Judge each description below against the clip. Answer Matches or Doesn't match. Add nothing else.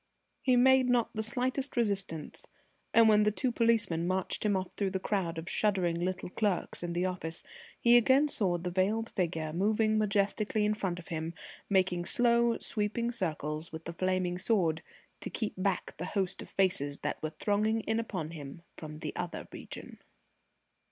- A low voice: Doesn't match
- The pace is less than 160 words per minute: Doesn't match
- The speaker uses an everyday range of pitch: Matches